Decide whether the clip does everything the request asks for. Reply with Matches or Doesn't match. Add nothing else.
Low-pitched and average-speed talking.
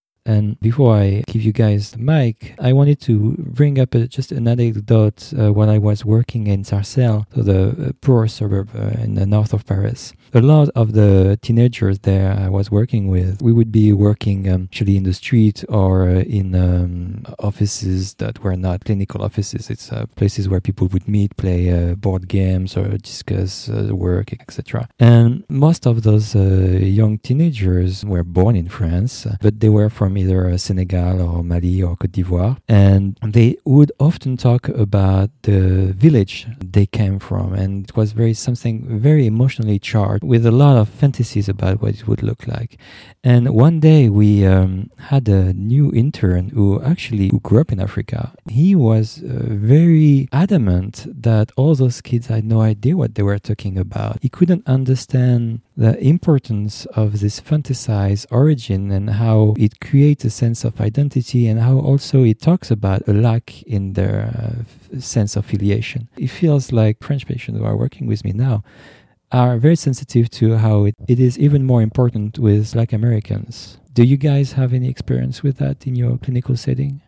Matches